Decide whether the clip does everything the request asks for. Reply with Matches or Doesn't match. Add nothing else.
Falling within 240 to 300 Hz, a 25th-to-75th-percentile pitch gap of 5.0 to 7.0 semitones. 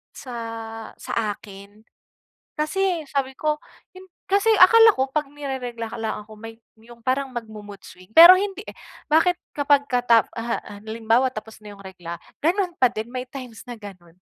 Matches